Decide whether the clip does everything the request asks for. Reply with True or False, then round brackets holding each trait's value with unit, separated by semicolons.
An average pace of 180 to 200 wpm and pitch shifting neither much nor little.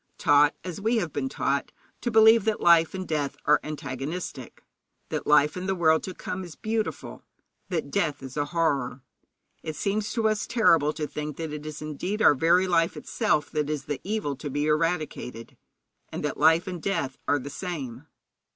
True (190 wpm; 4.4 semitones)